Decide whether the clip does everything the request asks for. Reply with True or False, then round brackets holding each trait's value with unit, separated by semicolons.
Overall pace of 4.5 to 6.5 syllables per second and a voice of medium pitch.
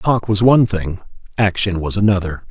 False (5.3 syllables/s; 100 Hz)